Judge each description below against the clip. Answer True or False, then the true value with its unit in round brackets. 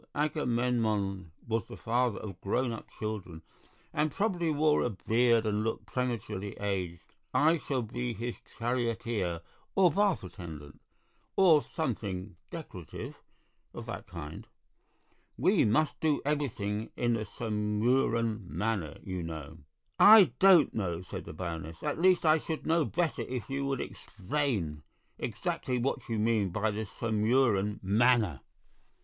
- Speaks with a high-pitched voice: False (115 Hz)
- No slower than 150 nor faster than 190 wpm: False (135 wpm)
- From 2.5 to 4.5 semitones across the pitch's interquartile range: False (5.6 semitones)